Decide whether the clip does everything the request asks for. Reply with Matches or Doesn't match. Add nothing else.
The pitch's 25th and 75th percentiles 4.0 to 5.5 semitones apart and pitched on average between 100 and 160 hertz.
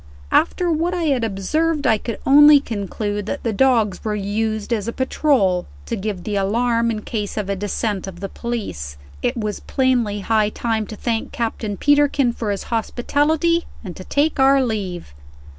Doesn't match